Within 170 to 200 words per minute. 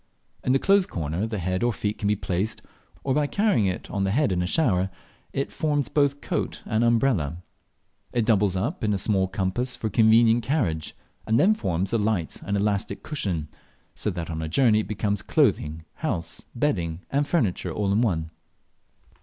Yes: average, 185 wpm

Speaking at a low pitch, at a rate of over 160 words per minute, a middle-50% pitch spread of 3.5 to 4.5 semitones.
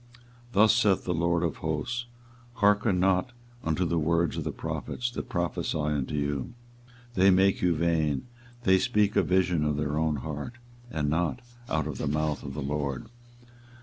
Yes: very low, 85 Hz; average, 175 wpm; average, 4.2 semitones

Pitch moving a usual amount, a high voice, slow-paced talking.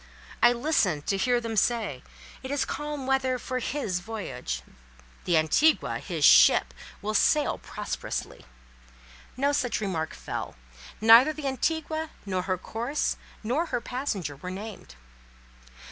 No: wide, 6.6 semitones; high, 240 Hz; slow, 130 wpm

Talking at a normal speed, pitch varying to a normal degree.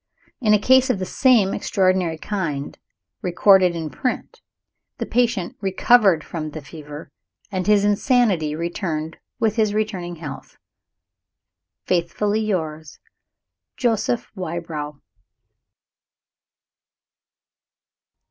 No: slow, 95 wpm; average, 4.9 semitones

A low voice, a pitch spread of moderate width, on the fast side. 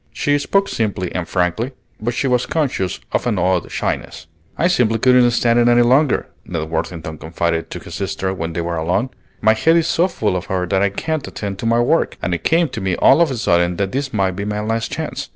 No: low, 105 Hz; wide, 5.9 semitones; fast, 235 wpm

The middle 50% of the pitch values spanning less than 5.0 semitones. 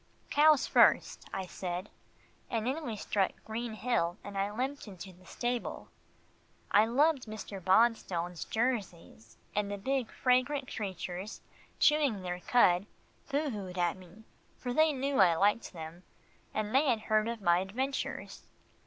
No: wide, 5.4 semitones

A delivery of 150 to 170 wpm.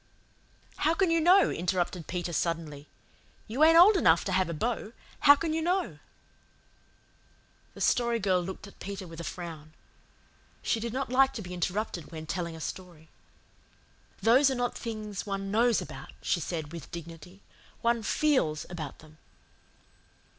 Yes: average, 160 wpm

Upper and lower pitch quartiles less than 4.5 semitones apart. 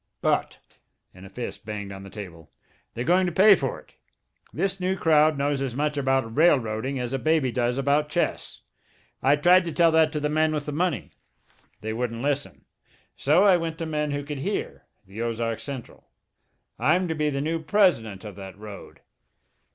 No: wide, 5.6 semitones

